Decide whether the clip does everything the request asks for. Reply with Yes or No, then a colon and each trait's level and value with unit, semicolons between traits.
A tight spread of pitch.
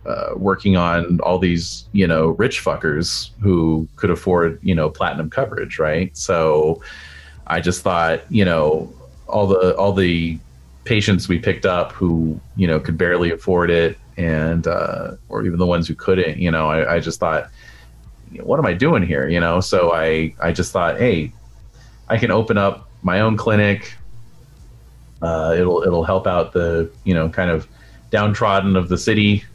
No: average, 3.2 semitones